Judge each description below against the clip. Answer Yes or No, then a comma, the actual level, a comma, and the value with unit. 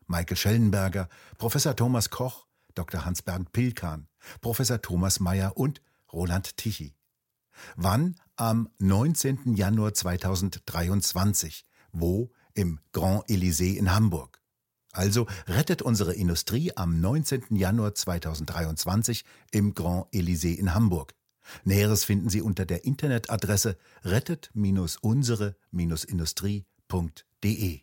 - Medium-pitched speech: No, low, 100 Hz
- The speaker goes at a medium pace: No, slow, 95 wpm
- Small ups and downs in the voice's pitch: No, average, 4.1 semitones